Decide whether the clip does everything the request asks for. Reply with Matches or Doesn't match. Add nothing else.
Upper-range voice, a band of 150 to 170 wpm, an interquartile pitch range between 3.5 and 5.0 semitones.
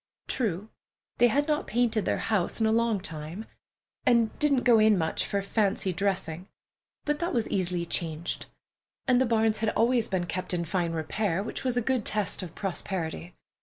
Doesn't match